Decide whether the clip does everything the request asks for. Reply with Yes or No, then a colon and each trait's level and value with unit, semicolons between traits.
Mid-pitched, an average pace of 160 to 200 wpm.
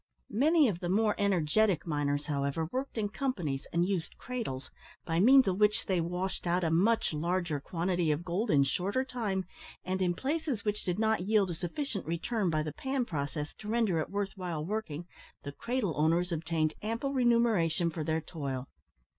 Yes: medium, 180 Hz; average, 180 wpm